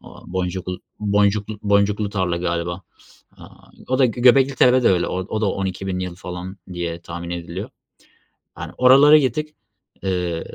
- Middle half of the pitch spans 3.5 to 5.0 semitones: Yes, average, 3.8 semitones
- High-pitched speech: No, very low, 95 Hz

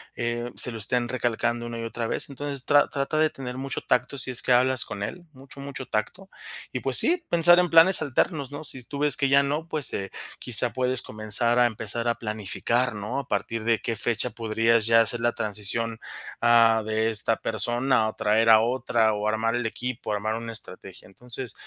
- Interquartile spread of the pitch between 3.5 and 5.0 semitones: No, average, 3.0 semitones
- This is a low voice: Yes, low, 120 Hz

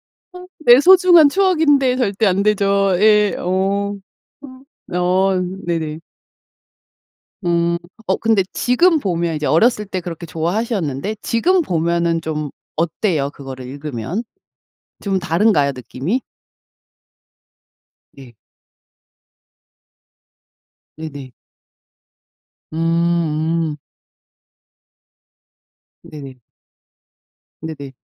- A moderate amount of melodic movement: No, wide, 5.7 semitones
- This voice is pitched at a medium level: Yes, medium, 180 Hz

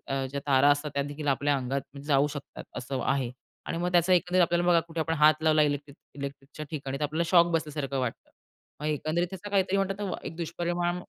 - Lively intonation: No, average, 3.6 semitones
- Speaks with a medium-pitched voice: Yes, medium, 155 Hz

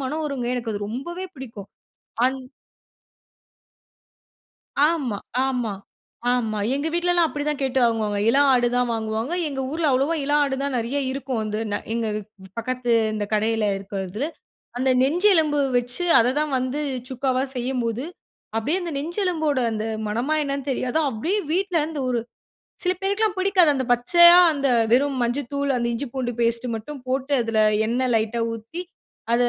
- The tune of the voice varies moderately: Yes, average, 4.2 semitones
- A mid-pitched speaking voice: No, very high, 260 Hz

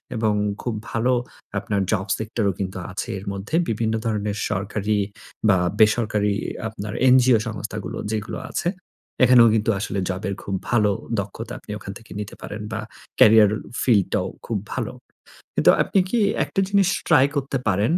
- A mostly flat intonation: Yes, narrow, 2.3 semitones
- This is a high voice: No, low, 110 Hz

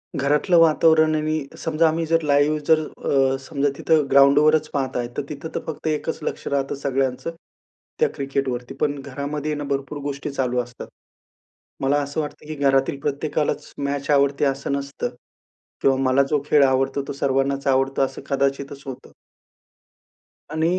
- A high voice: No, medium, 140 Hz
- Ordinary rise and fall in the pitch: No, narrow, 1.9 semitones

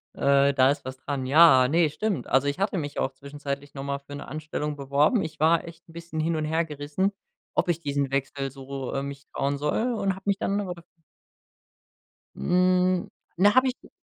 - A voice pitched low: No, medium, 150 Hz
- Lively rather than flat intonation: No, average, 3.9 semitones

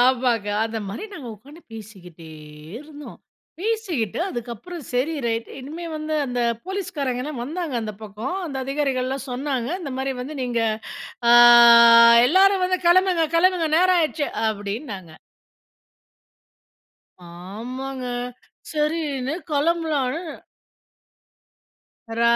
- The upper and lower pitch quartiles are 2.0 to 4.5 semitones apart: No, wide, 5.5 semitones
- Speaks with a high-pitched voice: Yes, very high, 275 Hz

